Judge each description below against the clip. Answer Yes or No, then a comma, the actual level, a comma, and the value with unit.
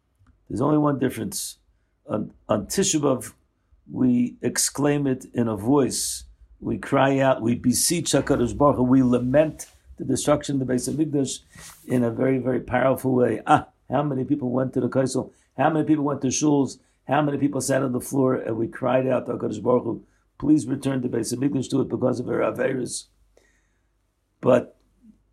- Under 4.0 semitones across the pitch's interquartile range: Yes, average, 2.9 semitones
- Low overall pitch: Yes, low, 130 Hz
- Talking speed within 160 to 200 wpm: Yes, average, 175 wpm